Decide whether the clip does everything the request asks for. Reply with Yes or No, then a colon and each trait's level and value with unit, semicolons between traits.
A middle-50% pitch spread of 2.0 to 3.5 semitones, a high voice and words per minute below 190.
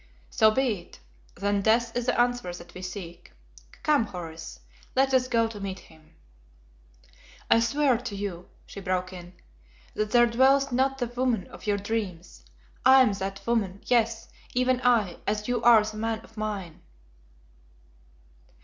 No: average, 4.1 semitones; high, 220 Hz; average, 160 wpm